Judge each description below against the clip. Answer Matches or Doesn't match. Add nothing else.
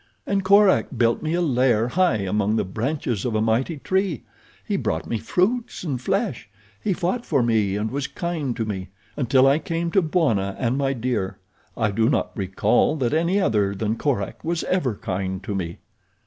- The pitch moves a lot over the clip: Matches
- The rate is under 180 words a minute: Doesn't match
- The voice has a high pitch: Doesn't match